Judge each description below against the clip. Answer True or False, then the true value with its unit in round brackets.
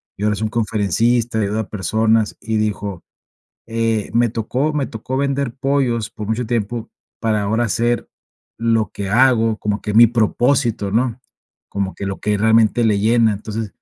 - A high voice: False (110 Hz)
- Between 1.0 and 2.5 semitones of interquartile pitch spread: True (2.1 semitones)